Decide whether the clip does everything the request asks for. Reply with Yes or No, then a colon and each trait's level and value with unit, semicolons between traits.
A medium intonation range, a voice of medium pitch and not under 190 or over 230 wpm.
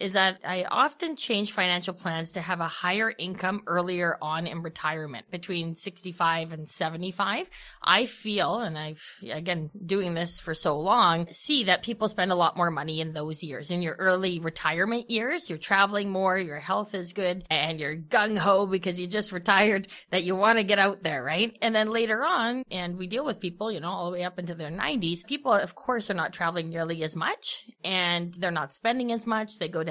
Yes: average, 3.6 semitones; medium, 180 Hz; fast, 205 wpm